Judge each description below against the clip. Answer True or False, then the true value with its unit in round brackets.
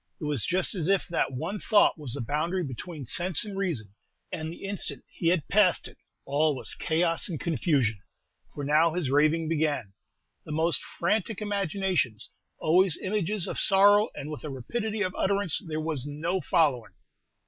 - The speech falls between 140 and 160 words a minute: False (170 wpm)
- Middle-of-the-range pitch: True (165 Hz)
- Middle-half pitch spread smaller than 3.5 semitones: False (4.4 semitones)